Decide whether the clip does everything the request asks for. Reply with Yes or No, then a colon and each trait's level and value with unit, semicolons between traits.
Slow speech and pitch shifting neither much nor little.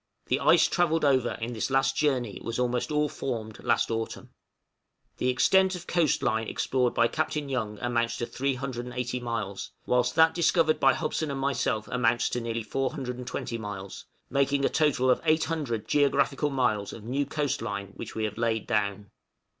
No: average, 170 wpm; average, 3.7 semitones